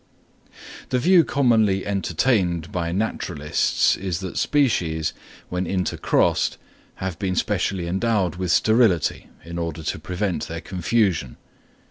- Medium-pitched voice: No, very low, 95 Hz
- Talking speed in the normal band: No, slow, 115 wpm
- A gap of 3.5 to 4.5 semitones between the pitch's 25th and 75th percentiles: Yes, average, 4.0 semitones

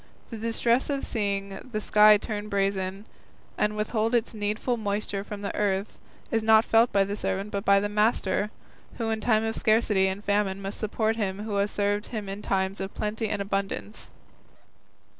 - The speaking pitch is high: Yes, high, 210 Hz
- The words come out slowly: No, average, 180 wpm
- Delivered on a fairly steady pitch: Yes, narrow, 1.7 semitones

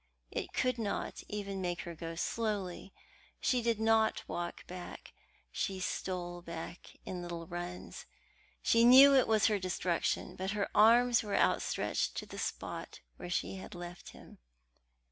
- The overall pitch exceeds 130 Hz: Yes, high, 190 Hz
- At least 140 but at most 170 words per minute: Yes, average, 150 wpm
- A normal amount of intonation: Yes, average, 4.0 semitones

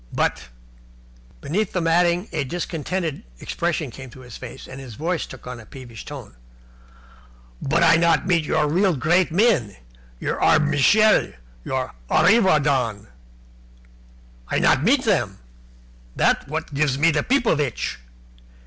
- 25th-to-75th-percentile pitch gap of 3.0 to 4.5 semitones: No, average, 5.3 semitones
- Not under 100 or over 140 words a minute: Yes, slow, 135 wpm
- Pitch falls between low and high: Yes, medium, 150 Hz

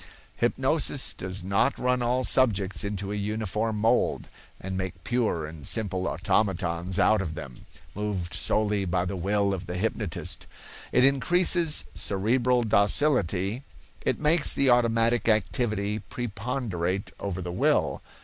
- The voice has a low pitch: Yes, low, 105 Hz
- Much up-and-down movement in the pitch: No, average, 4.3 semitones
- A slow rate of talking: Yes, slow, 130 wpm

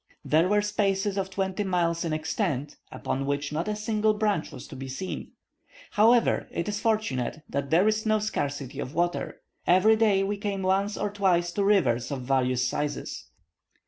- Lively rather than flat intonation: Yes, wide, 6.1 semitones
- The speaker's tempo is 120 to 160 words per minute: No, average, 175 wpm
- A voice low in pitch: No, high, 190 Hz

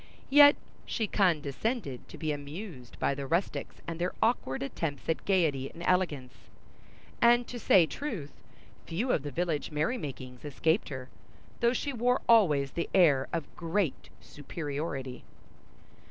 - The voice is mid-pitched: Yes, medium, 165 Hz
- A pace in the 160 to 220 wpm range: No, average, 140 wpm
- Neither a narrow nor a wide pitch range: No, wide, 6.6 semitones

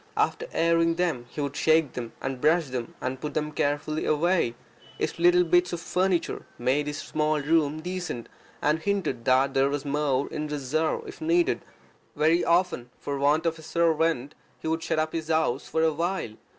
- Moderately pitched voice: Yes, medium, 155 Hz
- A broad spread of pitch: No, average, 3.0 semitones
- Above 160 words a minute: Yes, average, 190 wpm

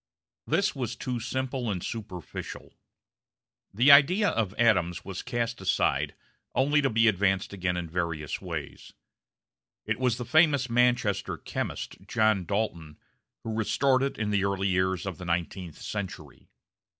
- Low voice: Yes, low, 110 Hz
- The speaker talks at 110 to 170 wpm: Yes, average, 140 wpm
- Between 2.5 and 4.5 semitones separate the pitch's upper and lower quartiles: No, average, 5.1 semitones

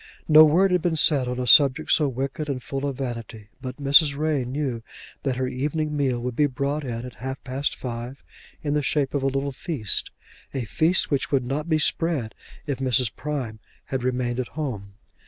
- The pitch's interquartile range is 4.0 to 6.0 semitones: No, average, 3.0 semitones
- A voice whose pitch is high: No, low, 135 Hz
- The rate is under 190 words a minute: No, average, 200 wpm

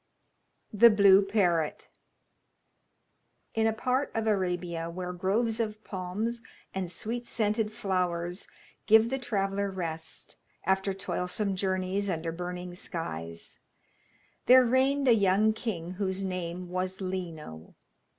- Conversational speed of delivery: No, slow, 115 wpm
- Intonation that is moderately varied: Yes, average, 3.4 semitones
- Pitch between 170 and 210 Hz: Yes, high, 190 Hz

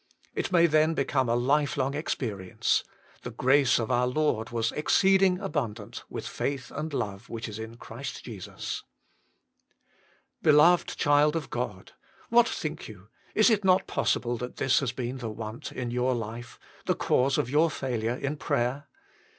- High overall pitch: No, low, 130 Hz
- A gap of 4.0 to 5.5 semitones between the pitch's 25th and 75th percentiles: Yes, average, 4.6 semitones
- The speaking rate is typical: Yes, average, 160 wpm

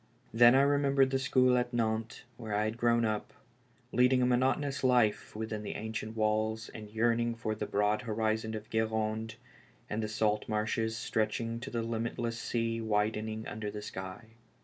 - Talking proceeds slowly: No, average, 175 wpm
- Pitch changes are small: Yes, narrow, 1.6 semitones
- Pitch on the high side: No, low, 110 Hz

